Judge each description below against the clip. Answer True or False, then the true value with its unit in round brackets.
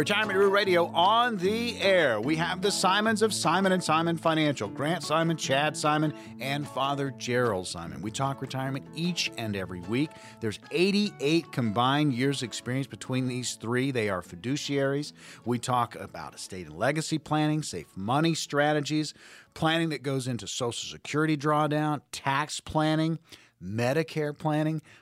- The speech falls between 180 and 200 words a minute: False (145 wpm)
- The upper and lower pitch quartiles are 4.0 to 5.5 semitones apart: True (4.5 semitones)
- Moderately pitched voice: True (150 Hz)